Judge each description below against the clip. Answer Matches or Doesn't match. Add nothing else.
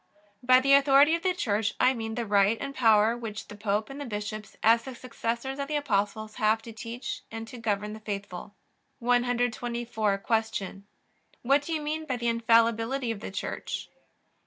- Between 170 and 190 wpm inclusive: Matches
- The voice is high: Matches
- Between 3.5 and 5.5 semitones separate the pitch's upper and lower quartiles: Doesn't match